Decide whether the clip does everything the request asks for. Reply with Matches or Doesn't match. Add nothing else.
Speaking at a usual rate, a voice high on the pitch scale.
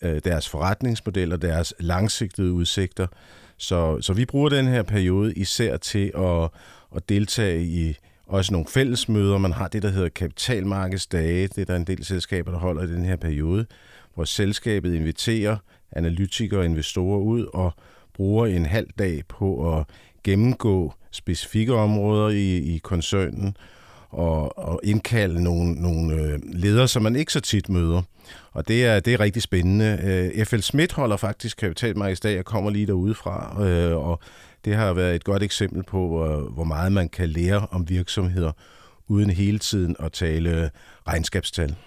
Doesn't match